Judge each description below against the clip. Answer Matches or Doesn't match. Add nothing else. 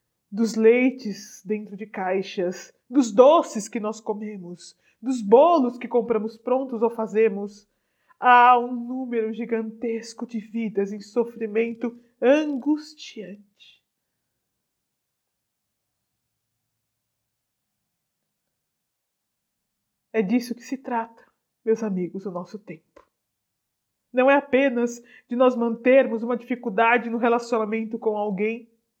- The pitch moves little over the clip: Doesn't match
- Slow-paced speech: Matches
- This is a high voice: Matches